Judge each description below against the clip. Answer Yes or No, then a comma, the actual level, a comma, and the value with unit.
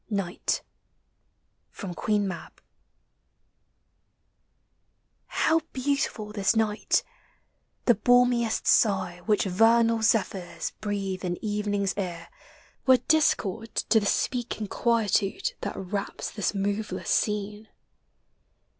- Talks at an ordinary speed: No, slow, 95 wpm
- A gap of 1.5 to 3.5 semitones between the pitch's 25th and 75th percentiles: Yes, narrow, 2.6 semitones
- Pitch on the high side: Yes, high, 210 Hz